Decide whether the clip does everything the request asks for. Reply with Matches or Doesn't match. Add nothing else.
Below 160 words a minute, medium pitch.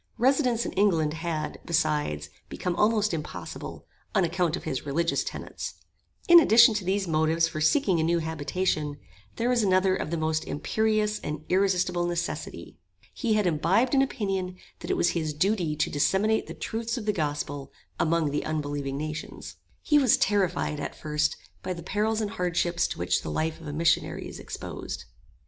Doesn't match